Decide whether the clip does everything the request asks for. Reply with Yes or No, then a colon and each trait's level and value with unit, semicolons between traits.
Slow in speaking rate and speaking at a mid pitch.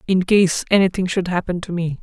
No: fast, 205 wpm; medium, 180 Hz